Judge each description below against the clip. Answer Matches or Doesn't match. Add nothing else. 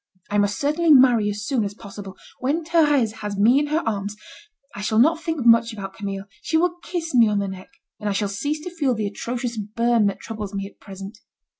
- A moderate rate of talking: Doesn't match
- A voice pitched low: Doesn't match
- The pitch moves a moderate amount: Doesn't match